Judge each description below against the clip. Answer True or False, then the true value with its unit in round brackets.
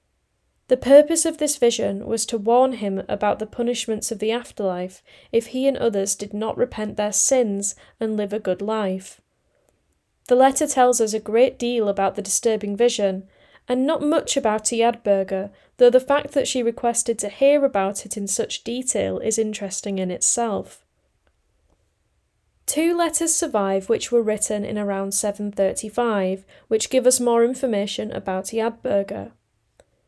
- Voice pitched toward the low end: False (225 Hz)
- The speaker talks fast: False (155 wpm)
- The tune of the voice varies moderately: True (3.7 semitones)